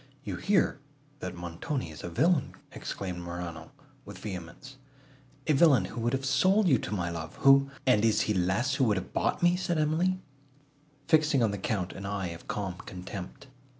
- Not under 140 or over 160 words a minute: No, average, 175 wpm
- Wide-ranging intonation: Yes, wide, 7.5 semitones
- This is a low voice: Yes, low, 120 Hz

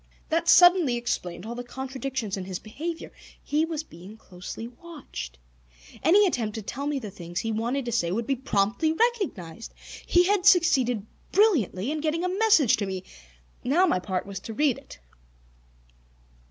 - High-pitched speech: Yes, very high, 250 Hz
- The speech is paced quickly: No, average, 165 wpm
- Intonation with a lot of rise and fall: Yes, wide, 7.9 semitones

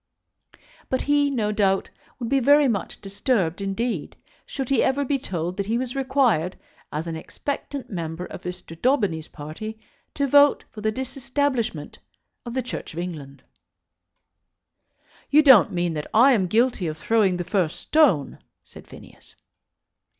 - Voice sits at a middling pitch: No, high, 220 Hz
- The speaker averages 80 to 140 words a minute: No, average, 150 wpm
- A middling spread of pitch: No, wide, 6.9 semitones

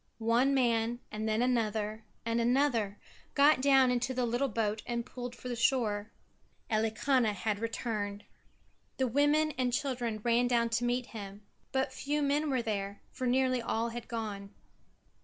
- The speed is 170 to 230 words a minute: No, average, 160 wpm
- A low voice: No, high, 235 Hz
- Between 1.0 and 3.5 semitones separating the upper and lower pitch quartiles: Yes, average, 2.8 semitones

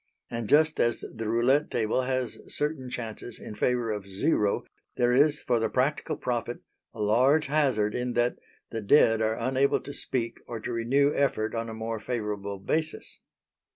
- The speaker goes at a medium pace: Yes, average, 170 wpm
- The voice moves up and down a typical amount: Yes, average, 3.3 semitones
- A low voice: Yes, low, 120 Hz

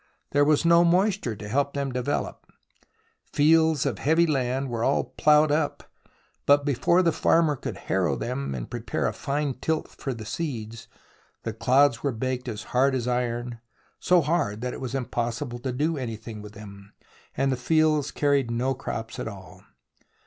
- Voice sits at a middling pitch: No, low, 130 Hz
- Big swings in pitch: No, average, 4.3 semitones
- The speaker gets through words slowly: No, average, 175 wpm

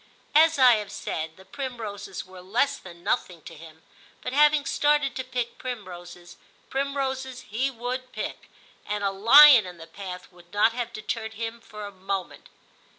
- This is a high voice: Yes, high, 220 Hz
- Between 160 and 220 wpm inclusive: Yes, average, 165 wpm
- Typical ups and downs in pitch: No, wide, 5.8 semitones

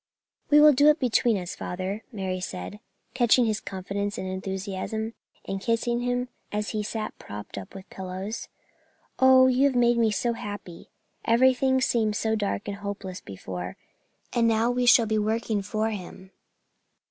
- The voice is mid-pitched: No, high, 215 Hz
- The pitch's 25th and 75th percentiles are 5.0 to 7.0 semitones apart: No, average, 3.8 semitones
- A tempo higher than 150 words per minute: Yes, average, 160 wpm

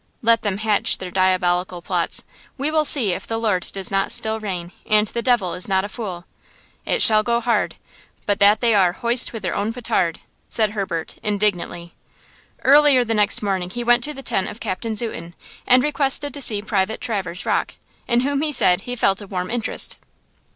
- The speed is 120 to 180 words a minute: No, average, 195 wpm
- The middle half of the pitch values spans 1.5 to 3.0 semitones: No, average, 4.1 semitones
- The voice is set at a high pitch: Yes, high, 210 Hz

